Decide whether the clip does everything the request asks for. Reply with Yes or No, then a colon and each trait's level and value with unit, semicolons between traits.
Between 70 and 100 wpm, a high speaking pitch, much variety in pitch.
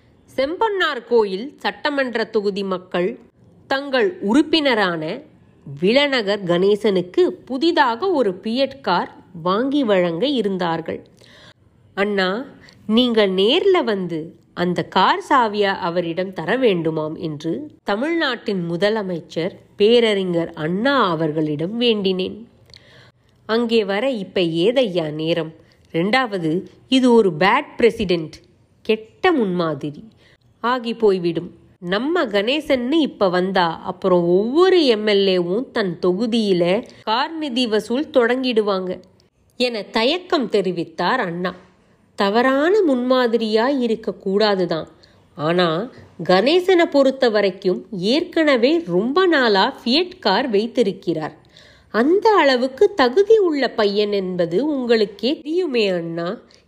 Yes: average, 90 wpm; high, 210 Hz; wide, 6.4 semitones